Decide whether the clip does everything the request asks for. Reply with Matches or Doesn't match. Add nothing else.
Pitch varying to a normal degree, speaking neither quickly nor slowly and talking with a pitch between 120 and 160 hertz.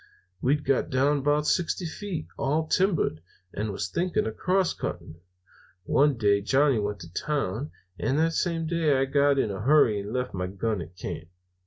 Doesn't match